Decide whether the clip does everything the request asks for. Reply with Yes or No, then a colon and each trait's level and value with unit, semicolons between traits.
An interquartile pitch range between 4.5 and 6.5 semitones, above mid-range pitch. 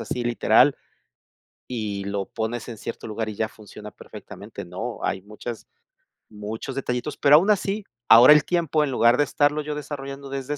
No: average, 5.1 semitones; low, 125 Hz